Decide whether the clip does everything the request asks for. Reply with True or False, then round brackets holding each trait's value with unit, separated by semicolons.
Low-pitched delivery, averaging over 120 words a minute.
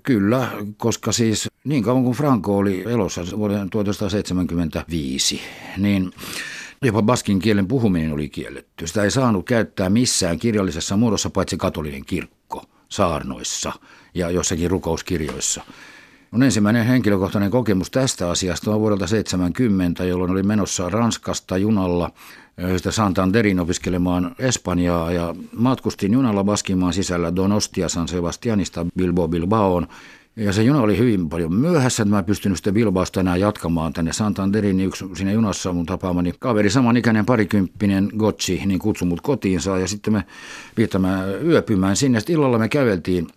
True (100 Hz; 140 wpm)